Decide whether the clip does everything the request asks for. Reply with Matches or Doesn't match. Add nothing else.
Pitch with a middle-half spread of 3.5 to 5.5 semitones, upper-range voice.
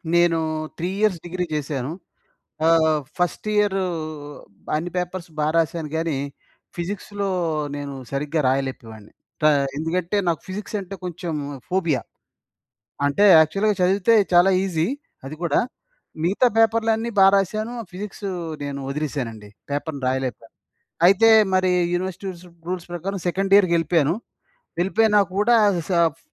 Doesn't match